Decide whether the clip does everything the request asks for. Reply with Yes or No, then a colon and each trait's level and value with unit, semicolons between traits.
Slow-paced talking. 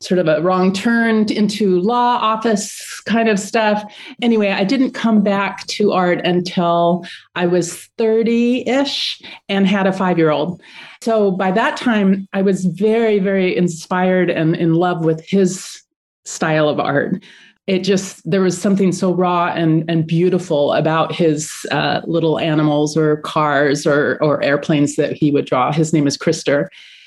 No: average, 165 wpm